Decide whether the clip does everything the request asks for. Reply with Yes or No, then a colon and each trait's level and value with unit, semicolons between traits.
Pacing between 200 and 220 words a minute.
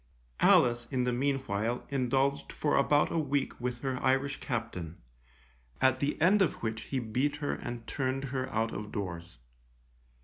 No: average, 160 wpm